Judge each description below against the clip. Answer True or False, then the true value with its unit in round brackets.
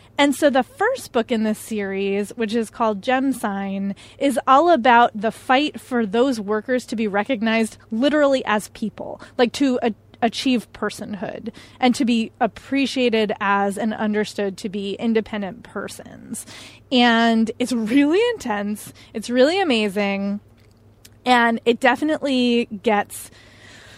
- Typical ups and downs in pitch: True (3.4 semitones)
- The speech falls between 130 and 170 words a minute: True (135 wpm)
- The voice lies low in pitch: False (230 Hz)